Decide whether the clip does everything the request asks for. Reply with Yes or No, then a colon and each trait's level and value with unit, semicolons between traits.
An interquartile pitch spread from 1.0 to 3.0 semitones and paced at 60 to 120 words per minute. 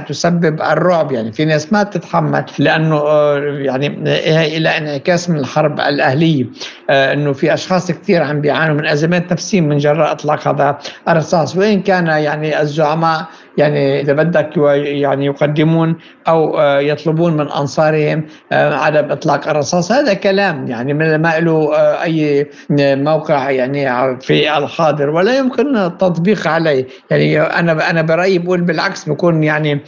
No: average, 2.7 semitones; fast, 135 wpm